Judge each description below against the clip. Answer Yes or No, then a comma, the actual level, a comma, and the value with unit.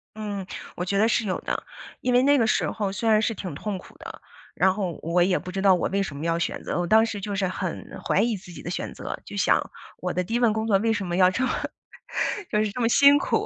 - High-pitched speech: Yes, high, 200 Hz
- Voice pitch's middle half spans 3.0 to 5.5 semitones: Yes, average, 3.5 semitones